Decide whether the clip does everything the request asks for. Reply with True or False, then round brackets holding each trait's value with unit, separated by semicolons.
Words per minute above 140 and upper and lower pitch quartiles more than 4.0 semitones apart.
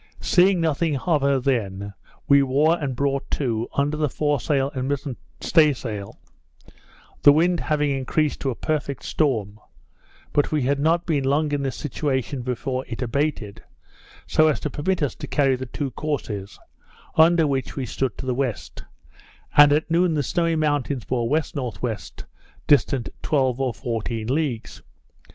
False (160 wpm; 3.2 semitones)